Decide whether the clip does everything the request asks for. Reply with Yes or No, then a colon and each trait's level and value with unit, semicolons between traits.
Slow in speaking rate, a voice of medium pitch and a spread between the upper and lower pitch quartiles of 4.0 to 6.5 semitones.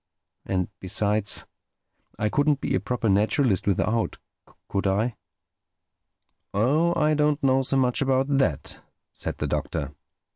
No: slow, 125 wpm; low, 120 Hz; wide, 5.6 semitones